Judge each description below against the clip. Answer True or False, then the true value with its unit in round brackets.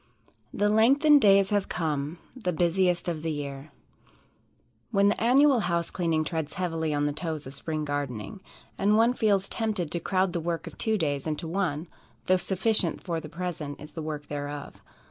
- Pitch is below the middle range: False (170 Hz)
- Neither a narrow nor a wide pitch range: True (4.7 semitones)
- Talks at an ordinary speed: True (180 wpm)